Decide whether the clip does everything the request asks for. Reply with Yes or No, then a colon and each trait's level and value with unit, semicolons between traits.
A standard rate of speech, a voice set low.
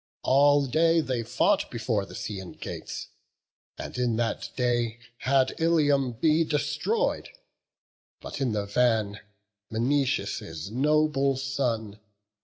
No: slow, 110 wpm; low, 130 Hz